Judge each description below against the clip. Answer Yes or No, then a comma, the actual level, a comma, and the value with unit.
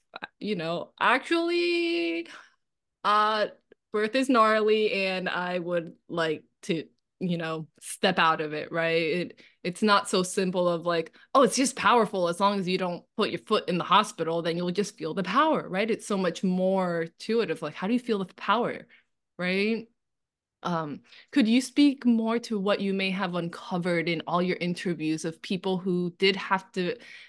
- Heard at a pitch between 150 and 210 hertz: Yes, high, 190 Hz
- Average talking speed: Yes, average, 185 wpm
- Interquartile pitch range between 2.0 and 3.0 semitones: No, average, 4.3 semitones